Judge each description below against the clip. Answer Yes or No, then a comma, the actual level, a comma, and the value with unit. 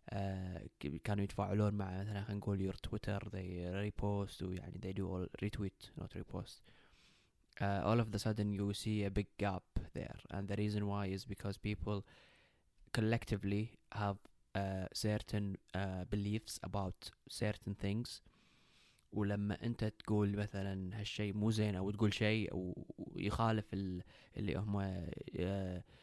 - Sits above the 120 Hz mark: No, low, 100 Hz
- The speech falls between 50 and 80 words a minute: No, fast, 135 wpm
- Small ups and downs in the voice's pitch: Yes, narrow, 1.6 semitones